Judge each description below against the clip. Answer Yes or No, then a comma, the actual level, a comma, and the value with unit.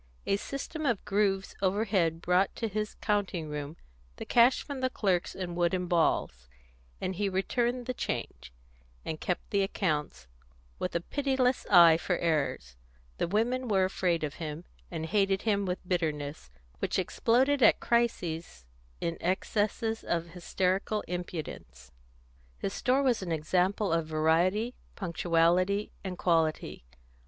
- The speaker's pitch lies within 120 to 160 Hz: No, medium, 185 Hz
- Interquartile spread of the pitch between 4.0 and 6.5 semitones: Yes, average, 4.3 semitones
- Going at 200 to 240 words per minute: No, average, 140 wpm